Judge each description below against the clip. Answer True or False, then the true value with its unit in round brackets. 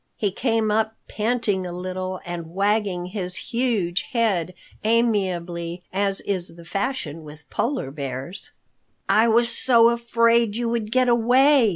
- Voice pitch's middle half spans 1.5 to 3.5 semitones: False (4.7 semitones)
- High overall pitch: True (205 Hz)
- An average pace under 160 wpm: True (140 wpm)